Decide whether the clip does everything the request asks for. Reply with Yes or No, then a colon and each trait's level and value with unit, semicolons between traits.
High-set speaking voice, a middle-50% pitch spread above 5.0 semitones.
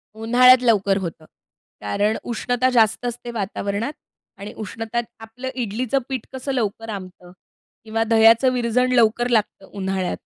No: high, 225 Hz; average, 3.3 semitones